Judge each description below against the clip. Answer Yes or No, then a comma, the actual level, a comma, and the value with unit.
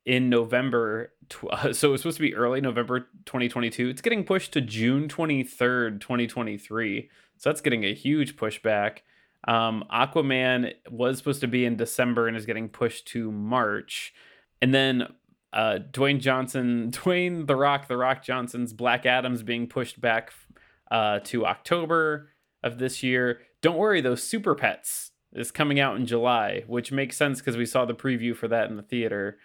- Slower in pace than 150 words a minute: No, average, 165 wpm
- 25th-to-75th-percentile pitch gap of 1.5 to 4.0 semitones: Yes, narrow, 2.6 semitones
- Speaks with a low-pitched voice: Yes, low, 125 Hz